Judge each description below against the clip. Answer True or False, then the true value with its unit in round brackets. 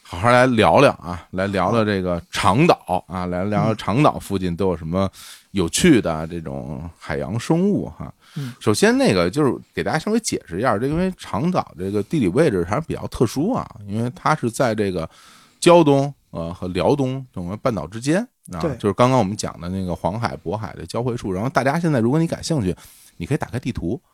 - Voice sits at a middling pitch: False (110 Hz)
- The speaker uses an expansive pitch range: True (7.0 semitones)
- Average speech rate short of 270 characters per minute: False (315 characters per minute)